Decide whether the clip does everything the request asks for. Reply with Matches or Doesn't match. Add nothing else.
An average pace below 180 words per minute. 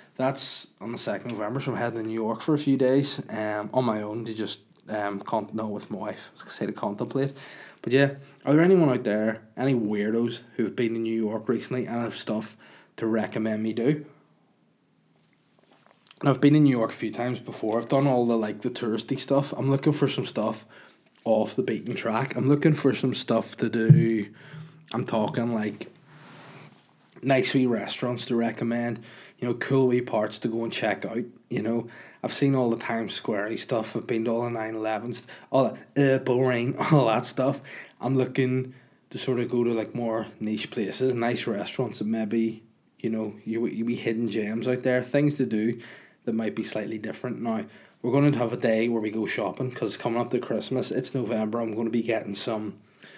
Doesn't match